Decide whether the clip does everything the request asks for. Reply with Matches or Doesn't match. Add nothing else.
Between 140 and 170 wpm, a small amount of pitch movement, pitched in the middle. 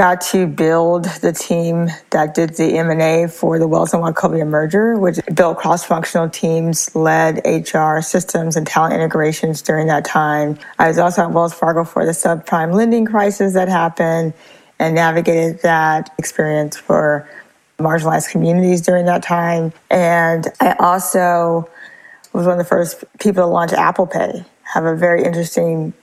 Matches